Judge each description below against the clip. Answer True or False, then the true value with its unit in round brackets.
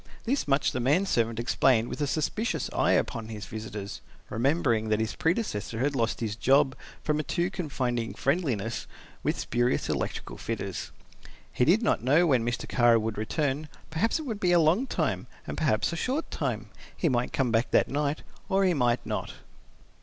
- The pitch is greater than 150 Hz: False (135 Hz)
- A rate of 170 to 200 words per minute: True (185 wpm)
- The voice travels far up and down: True (6.1 semitones)